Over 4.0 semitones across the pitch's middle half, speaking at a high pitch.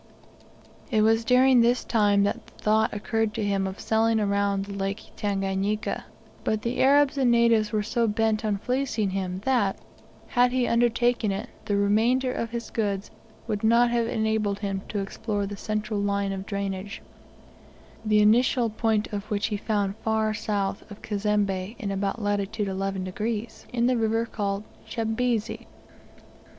No: narrow, 2.4 semitones; high, 215 Hz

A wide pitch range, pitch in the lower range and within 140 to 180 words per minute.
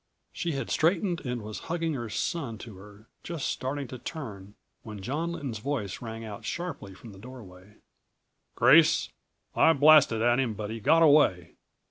Yes: wide, 6.3 semitones; low, 125 Hz; average, 165 wpm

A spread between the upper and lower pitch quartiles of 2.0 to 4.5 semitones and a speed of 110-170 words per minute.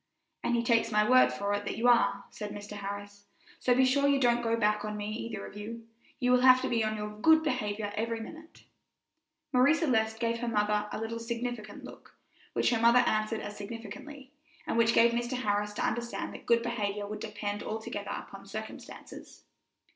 No: narrow, 2.4 semitones; average, 200 wpm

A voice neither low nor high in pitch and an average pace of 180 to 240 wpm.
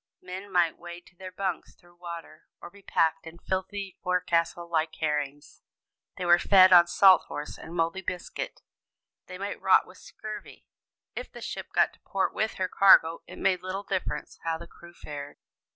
Yes: medium, 175 Hz; average, 185 wpm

